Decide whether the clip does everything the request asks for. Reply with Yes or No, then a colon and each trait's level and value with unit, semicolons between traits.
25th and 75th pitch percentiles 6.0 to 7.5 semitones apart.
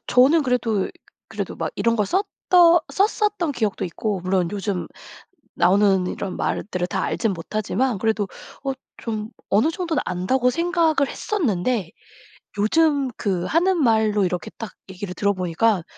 Yes: wide, 7.2 semitones